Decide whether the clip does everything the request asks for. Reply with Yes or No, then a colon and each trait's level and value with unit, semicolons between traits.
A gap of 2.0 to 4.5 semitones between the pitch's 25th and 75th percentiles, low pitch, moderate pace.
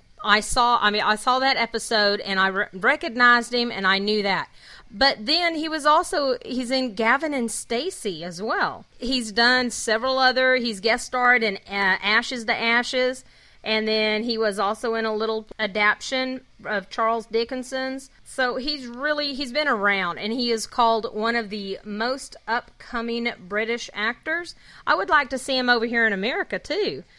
No: average, 3.3 semitones; high, 235 Hz; average, 180 wpm